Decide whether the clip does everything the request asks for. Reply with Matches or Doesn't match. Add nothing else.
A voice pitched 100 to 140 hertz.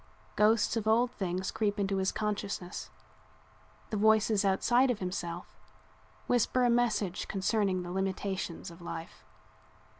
Doesn't match